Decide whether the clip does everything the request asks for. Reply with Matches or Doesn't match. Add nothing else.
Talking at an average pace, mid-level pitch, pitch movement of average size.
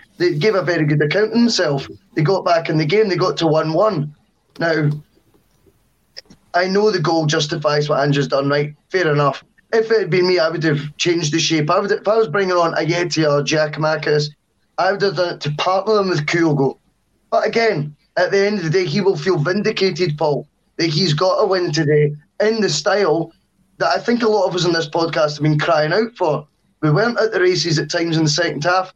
Doesn't match